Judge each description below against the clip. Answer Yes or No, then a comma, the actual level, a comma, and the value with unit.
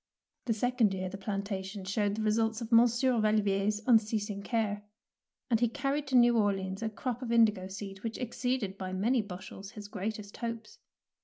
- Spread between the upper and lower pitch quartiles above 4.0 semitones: No, average, 2.8 semitones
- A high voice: Yes, high, 215 Hz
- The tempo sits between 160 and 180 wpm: Yes, average, 175 wpm